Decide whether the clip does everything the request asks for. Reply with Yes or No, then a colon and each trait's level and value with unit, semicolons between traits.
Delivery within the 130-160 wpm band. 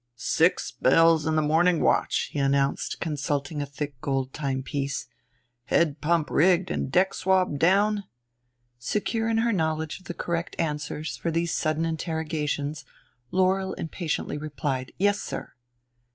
Yes: average, 140 wpm